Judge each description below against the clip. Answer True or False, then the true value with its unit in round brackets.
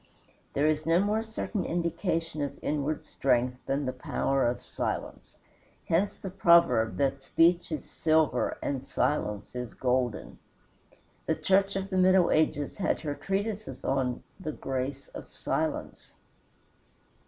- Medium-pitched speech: True (155 Hz)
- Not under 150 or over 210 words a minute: False (135 wpm)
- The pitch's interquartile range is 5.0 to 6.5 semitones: True (5.4 semitones)